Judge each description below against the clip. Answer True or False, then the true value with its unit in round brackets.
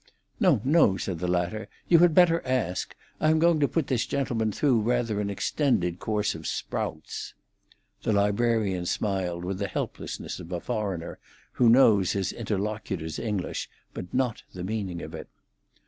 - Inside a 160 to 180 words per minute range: True (165 wpm)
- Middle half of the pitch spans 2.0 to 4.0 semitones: False (5.4 semitones)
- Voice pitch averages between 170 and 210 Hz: False (105 Hz)